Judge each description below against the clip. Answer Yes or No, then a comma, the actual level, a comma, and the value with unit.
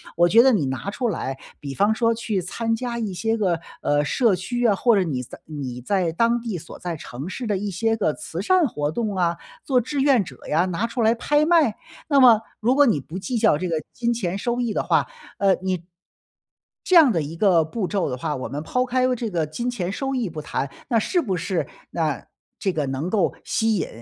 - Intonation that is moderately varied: No, wide, 6.1 semitones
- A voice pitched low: No, high, 200 Hz